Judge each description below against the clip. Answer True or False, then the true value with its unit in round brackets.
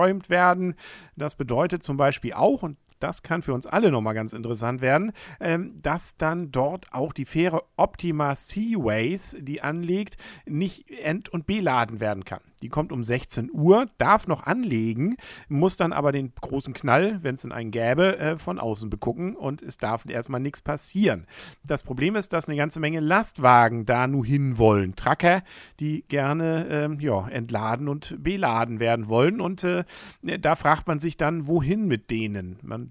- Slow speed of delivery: False (165 wpm)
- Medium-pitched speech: True (150 Hz)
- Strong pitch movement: True (6.1 semitones)